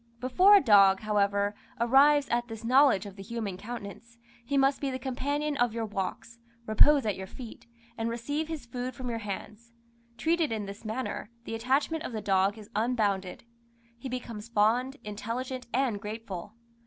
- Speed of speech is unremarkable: Yes, average, 170 wpm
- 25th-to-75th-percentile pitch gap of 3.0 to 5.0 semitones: Yes, average, 3.9 semitones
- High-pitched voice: Yes, high, 230 Hz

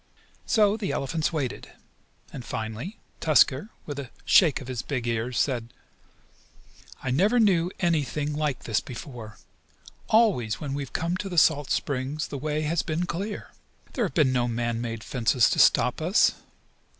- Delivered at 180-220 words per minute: No, average, 160 wpm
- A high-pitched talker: No, medium, 145 Hz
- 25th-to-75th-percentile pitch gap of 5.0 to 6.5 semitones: Yes, wide, 5.4 semitones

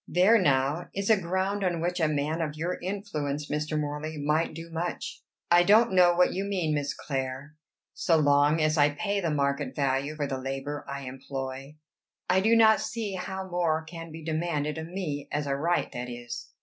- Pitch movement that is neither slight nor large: Yes, average, 3.8 semitones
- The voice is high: No, medium, 155 Hz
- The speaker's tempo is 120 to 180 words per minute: No, average, 195 wpm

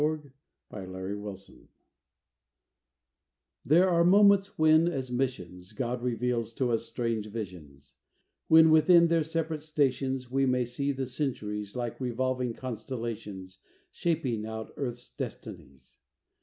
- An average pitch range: No, wide, 5.7 semitones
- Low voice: Yes, low, 125 Hz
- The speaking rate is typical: No, slow, 125 wpm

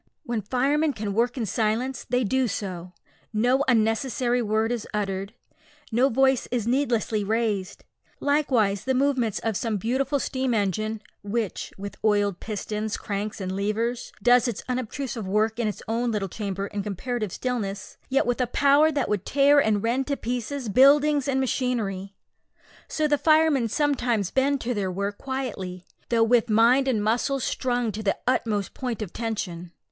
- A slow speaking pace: No, average, 160 wpm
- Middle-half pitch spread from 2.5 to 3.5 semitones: No, average, 3.9 semitones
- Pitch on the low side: No, high, 230 Hz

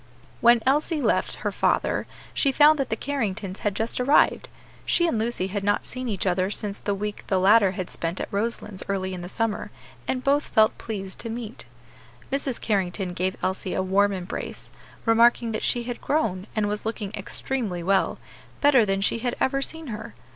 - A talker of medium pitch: No, high, 215 Hz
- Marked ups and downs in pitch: No, average, 4.1 semitones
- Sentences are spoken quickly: No, average, 190 wpm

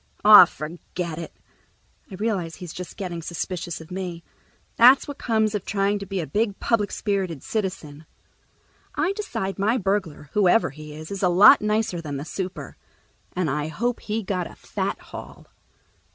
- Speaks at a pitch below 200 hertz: Yes, high, 190 Hz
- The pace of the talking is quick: No, average, 165 wpm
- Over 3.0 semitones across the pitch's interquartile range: Yes, average, 3.9 semitones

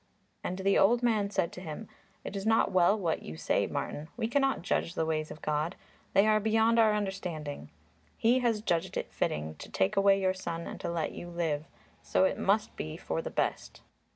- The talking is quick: Yes, fast, 210 wpm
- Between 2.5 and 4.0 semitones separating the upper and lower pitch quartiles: No, average, 4.7 semitones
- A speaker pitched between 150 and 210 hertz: Yes, high, 190 Hz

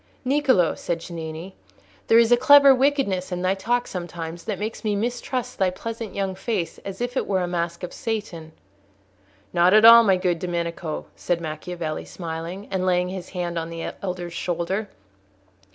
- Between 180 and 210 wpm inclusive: No, average, 170 wpm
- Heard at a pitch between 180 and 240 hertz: Yes, medium, 185 Hz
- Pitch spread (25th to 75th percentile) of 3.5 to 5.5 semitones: Yes, average, 4.5 semitones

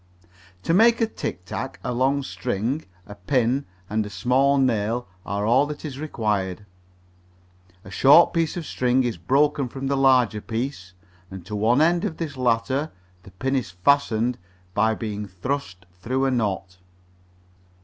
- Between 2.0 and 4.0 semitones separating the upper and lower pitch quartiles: No, average, 5.2 semitones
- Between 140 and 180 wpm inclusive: Yes, average, 160 wpm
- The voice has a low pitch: Yes, low, 125 Hz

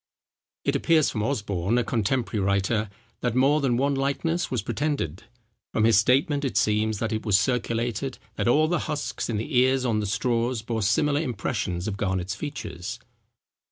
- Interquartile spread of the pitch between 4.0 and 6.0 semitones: Yes, average, 4.4 semitones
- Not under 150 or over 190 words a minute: Yes, average, 170 wpm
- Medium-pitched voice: No, low, 115 Hz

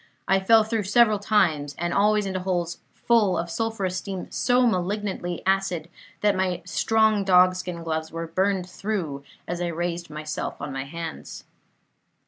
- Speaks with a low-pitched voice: No, medium, 185 Hz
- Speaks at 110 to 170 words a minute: Yes, average, 150 wpm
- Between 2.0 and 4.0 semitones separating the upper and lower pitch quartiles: Yes, average, 3.4 semitones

